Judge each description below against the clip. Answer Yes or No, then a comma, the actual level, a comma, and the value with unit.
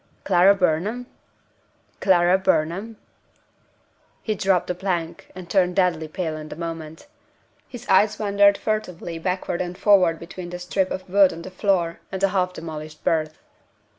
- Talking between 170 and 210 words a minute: No, average, 150 wpm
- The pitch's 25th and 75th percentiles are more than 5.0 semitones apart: No, average, 2.7 semitones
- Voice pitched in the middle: Yes, medium, 180 Hz